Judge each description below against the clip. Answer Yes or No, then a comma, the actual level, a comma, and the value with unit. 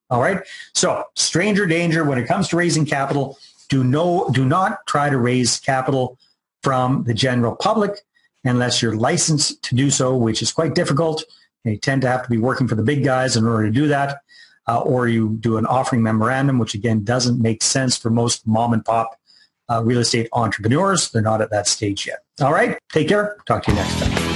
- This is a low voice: Yes, low, 125 Hz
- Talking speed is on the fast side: Yes, fast, 210 wpm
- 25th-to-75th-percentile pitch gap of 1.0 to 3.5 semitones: No, average, 4.2 semitones